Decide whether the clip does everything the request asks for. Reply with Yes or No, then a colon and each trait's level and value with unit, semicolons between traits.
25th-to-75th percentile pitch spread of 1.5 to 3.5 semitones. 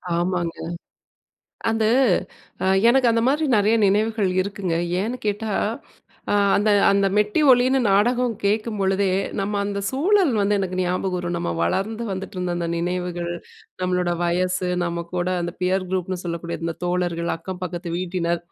Yes: average, 3.1 semitones